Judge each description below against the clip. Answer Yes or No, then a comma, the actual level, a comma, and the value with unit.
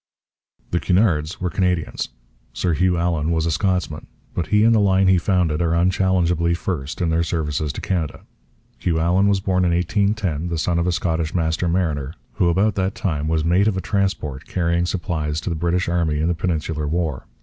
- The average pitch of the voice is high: No, very low, 85 Hz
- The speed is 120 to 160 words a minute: No, average, 195 wpm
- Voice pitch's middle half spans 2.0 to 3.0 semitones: Yes, narrow, 2.5 semitones